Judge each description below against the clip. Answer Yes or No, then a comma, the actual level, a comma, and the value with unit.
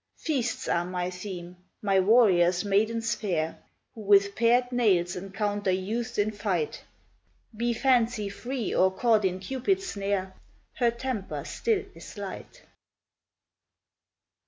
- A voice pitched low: No, high, 205 Hz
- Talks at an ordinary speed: No, slow, 120 wpm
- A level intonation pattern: No, average, 4.1 semitones